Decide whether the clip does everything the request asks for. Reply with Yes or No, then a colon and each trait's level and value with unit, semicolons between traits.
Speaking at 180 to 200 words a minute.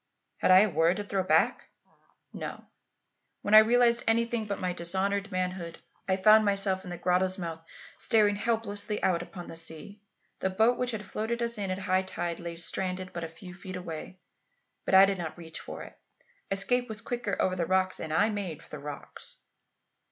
Yes: average, 195 wpm